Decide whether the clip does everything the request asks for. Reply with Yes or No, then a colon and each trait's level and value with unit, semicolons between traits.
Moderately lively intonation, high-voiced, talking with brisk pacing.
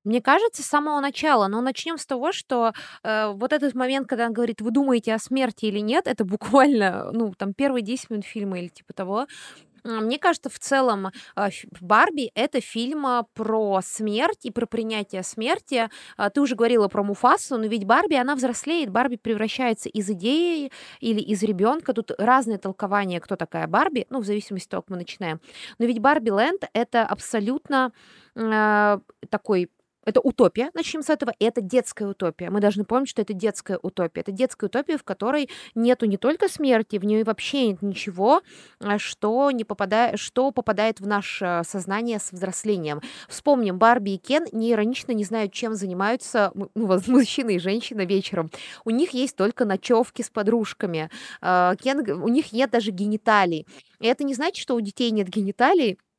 Yes: average, 4.0 semitones; high, 225 Hz; fast, 175 wpm